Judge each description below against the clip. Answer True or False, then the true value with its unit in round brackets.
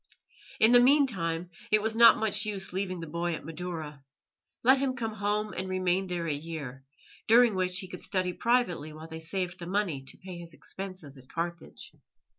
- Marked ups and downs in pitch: False (4.1 semitones)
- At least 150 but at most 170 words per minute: False (190 wpm)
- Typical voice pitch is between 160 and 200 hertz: True (185 Hz)